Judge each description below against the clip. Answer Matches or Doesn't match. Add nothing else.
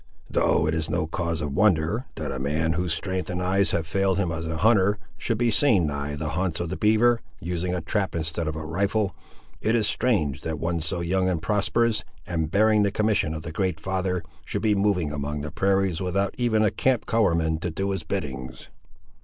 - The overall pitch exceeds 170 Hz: Doesn't match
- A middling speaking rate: Doesn't match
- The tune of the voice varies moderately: Matches